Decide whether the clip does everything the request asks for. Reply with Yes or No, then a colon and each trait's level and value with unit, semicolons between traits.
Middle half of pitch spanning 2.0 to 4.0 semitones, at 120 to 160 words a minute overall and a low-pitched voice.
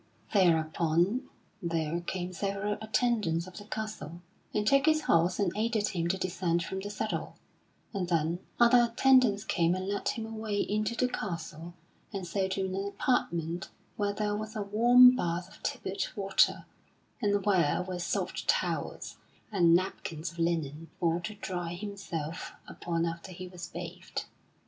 No: average, 3.7 semitones; average, 155 wpm; high, 190 Hz